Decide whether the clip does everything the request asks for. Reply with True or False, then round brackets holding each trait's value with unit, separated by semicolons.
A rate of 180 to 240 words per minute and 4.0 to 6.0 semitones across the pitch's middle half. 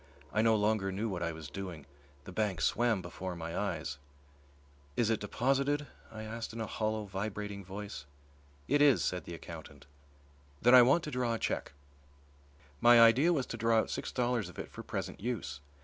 True (185 wpm; 4.3 semitones)